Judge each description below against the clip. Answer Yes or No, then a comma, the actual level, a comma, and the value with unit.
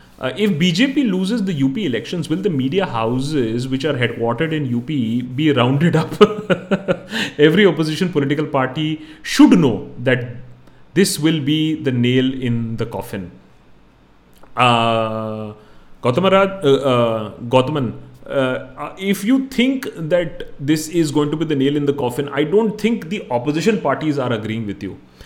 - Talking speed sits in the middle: Yes, average, 155 wpm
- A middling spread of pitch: No, wide, 6.7 semitones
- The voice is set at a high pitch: No, medium, 145 Hz